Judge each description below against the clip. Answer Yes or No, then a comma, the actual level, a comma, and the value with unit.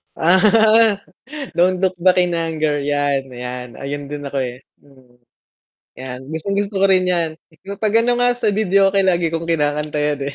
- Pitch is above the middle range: No, medium, 165 Hz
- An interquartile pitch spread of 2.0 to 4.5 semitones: No, average, 5.3 semitones